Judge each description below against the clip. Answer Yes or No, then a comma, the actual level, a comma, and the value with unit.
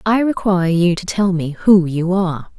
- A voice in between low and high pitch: Yes, medium, 180 Hz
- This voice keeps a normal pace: No, fast, 210 wpm